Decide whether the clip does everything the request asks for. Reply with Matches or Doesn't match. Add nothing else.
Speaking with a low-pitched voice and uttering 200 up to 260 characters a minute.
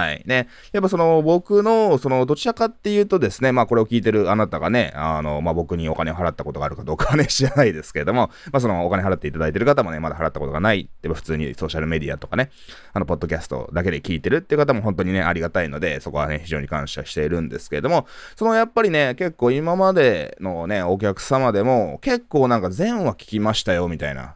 Doesn't match